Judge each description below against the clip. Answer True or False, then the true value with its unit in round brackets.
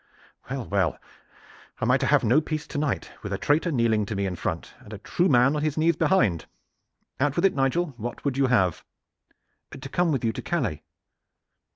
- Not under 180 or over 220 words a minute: True (205 wpm)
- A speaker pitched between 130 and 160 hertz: True (135 Hz)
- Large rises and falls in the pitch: True (6.3 semitones)